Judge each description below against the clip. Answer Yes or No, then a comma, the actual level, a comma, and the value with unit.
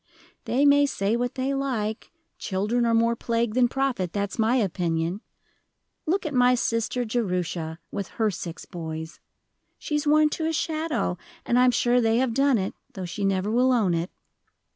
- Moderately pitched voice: No, high, 230 Hz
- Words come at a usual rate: Yes, average, 175 wpm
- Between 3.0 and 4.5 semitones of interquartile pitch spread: No, average, 5.2 semitones